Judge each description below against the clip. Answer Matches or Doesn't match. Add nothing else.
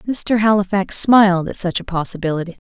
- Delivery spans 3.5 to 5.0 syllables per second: Doesn't match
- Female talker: Matches